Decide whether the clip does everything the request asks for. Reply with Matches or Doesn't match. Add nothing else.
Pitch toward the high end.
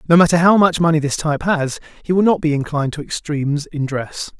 Doesn't match